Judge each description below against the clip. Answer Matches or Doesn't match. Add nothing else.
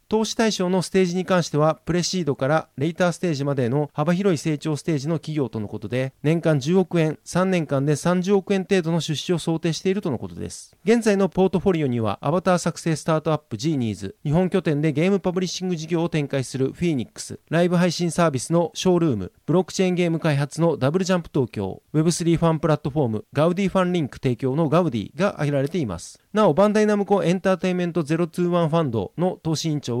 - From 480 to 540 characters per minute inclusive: Matches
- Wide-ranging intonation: Doesn't match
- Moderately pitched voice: Matches